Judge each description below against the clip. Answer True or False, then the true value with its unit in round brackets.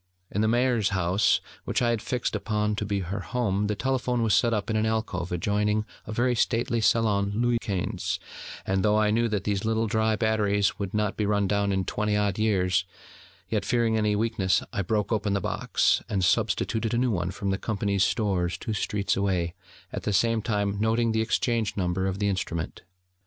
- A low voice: True (105 Hz)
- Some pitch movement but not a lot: False (2.2 semitones)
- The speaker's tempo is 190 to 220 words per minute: True (200 wpm)